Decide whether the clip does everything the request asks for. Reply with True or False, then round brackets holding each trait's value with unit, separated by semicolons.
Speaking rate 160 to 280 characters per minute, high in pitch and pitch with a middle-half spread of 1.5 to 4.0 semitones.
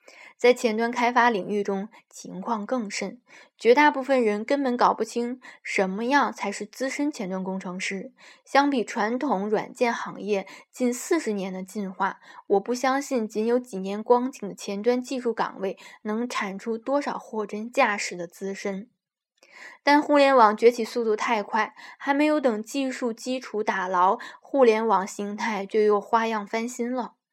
True (240 characters per minute; 225 Hz; 3.7 semitones)